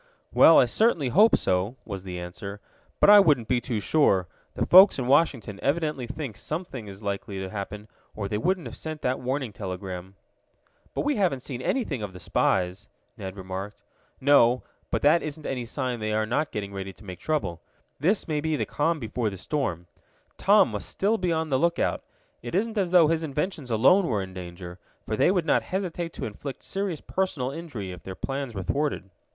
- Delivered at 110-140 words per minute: No, average, 200 wpm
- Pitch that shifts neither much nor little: No, wide, 8.1 semitones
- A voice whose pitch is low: Yes, low, 125 Hz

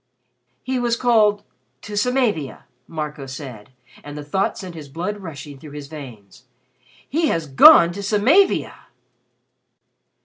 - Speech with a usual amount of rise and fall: No, wide, 6.6 semitones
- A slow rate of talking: Yes, slow, 130 wpm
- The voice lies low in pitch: No, medium, 165 Hz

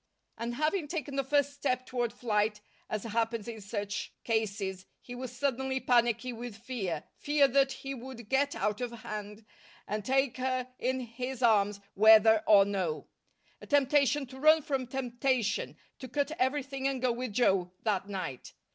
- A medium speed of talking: Yes, average, 165 wpm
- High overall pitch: Yes, high, 245 Hz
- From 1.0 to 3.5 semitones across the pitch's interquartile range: No, average, 3.9 semitones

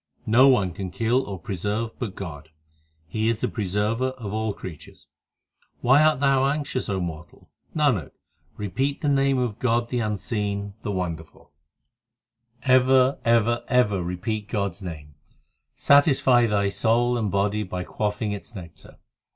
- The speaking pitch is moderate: No, low, 110 Hz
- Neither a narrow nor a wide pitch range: Yes, average, 4.3 semitones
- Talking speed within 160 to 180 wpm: No, average, 145 wpm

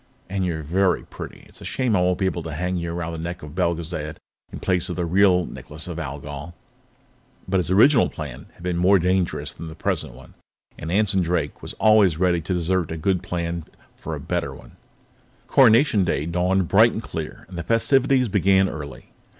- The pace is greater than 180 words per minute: Yes, average, 200 wpm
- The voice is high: No, very low, 90 Hz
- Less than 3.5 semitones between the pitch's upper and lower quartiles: Yes, average, 2.7 semitones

